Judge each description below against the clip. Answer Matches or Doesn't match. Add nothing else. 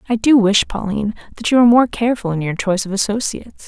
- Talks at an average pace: Doesn't match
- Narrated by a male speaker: Doesn't match